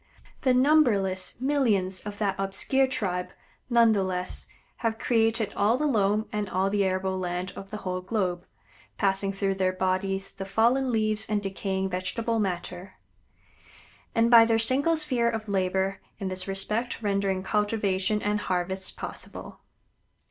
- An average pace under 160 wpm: Yes, average, 150 wpm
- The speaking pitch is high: Yes, high, 200 Hz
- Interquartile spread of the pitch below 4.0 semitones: Yes, average, 3.1 semitones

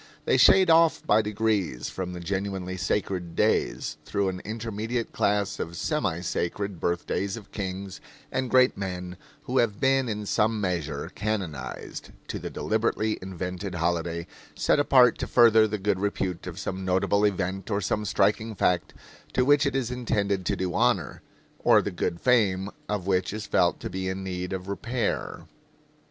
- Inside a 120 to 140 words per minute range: No, average, 165 wpm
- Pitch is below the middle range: Yes, low, 100 Hz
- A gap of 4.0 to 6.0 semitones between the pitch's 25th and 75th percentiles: No, average, 3.1 semitones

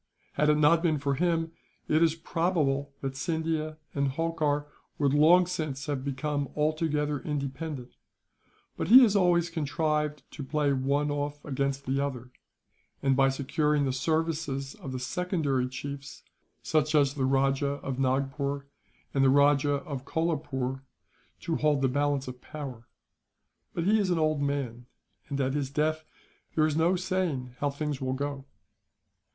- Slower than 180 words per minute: Yes, average, 155 wpm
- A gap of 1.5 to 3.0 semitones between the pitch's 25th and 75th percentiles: Yes, narrow, 2.5 semitones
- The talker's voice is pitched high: No, medium, 145 Hz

